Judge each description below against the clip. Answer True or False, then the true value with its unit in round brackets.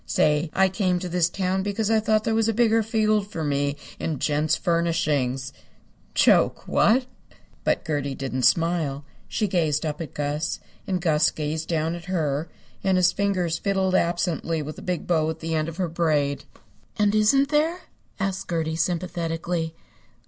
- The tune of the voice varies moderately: True (3.9 semitones)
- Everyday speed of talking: True (170 wpm)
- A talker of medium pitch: True (170 Hz)